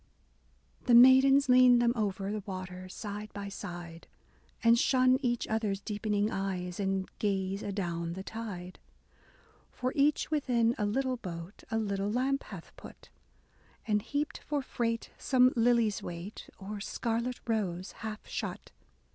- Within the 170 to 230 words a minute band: No, average, 140 wpm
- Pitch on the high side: Yes, high, 215 Hz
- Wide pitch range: No, average, 4.0 semitones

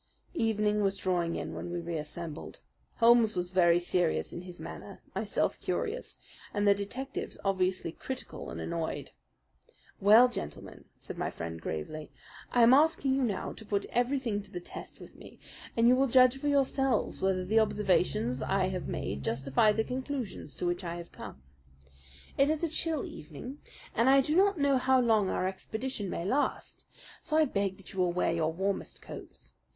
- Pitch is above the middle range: Yes, high, 205 Hz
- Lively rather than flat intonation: Yes, wide, 6.7 semitones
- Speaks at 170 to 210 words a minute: Yes, average, 175 wpm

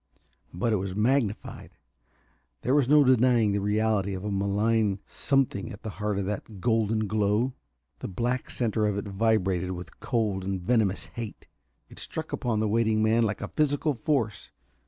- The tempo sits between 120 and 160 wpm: No, average, 170 wpm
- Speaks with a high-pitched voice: No, low, 110 Hz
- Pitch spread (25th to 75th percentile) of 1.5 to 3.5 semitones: Yes, average, 2.9 semitones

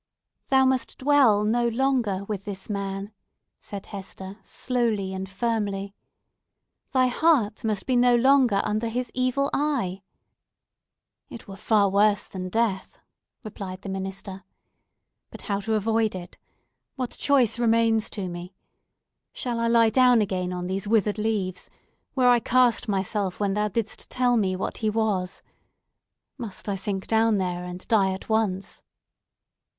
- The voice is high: Yes, high, 210 Hz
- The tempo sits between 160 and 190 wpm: No, average, 145 wpm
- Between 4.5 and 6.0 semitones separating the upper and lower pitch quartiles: No, average, 3.5 semitones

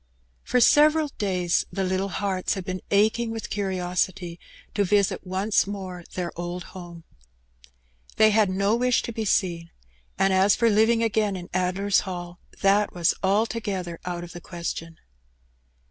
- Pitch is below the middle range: No, high, 190 Hz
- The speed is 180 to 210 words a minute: No, average, 150 wpm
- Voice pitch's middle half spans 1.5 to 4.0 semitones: Yes, average, 2.9 semitones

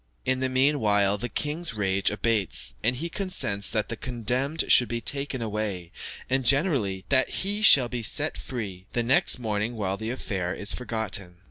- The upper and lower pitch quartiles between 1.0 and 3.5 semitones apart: No, average, 4.5 semitones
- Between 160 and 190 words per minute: Yes, average, 170 wpm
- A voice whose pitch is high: No, low, 115 Hz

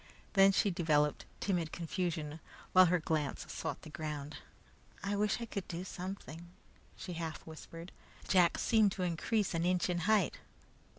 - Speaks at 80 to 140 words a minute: No, average, 155 wpm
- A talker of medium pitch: Yes, medium, 175 Hz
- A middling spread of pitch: Yes, average, 3.3 semitones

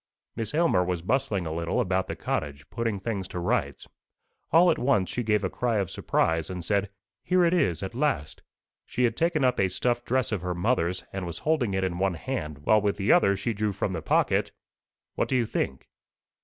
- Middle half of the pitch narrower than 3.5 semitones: No, wide, 5.4 semitones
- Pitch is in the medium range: No, low, 100 Hz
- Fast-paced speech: Yes, fast, 215 wpm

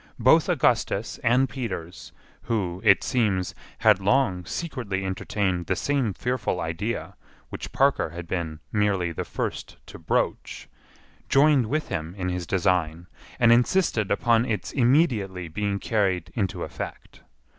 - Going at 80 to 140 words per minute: Yes, slow, 135 wpm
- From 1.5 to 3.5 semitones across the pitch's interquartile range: No, average, 5.1 semitones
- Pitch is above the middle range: No, low, 100 Hz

